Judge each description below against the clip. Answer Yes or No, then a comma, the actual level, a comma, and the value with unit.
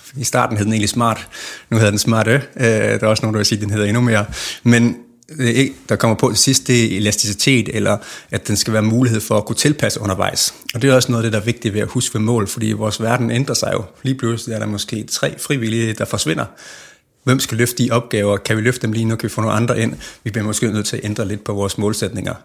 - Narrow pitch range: Yes, narrow, 2.1 semitones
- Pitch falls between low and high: No, low, 115 Hz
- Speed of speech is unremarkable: No, fast, 275 wpm